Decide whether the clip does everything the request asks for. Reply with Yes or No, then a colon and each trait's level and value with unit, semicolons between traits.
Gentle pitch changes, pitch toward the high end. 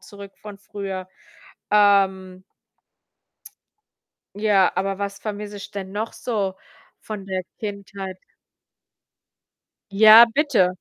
Yes: narrow, 1.5 semitones; high, 200 Hz